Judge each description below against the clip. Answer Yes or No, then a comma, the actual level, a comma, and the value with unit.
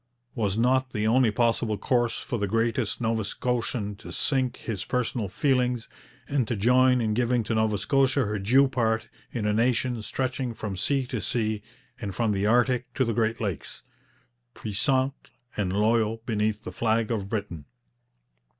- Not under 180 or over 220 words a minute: No, average, 165 wpm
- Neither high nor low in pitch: No, low, 115 Hz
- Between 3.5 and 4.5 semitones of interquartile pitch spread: No, average, 3.0 semitones